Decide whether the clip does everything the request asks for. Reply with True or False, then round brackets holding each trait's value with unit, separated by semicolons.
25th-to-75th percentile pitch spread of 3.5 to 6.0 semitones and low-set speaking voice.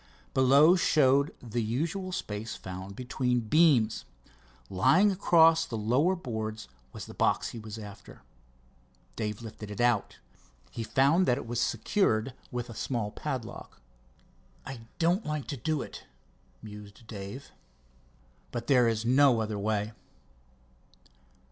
True (5.0 semitones; 120 Hz)